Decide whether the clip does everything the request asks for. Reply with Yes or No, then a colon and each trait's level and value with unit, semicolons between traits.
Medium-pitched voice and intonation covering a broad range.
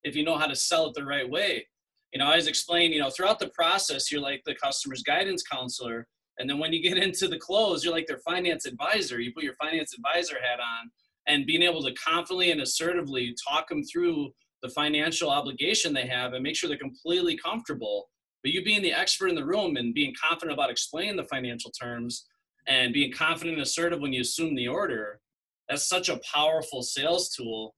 Yes: medium, 160 Hz; wide, 6.4 semitones